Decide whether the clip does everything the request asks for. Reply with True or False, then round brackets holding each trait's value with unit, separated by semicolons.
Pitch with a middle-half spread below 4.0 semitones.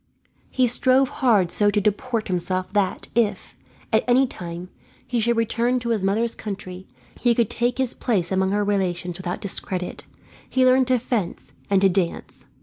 False (4.5 semitones)